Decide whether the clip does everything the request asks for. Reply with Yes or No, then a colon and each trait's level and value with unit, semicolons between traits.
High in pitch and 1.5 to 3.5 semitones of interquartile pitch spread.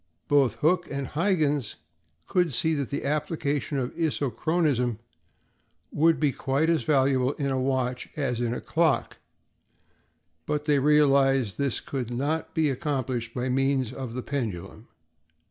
No: medium, 140 Hz; average, 2.9 semitones